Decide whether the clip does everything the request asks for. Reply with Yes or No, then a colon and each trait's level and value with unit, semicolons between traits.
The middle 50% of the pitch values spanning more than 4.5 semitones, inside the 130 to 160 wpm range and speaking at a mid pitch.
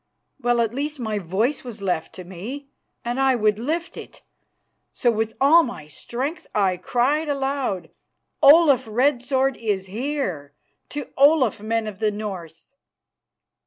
No: average, 5.2 semitones; average, 145 wpm; high, 240 Hz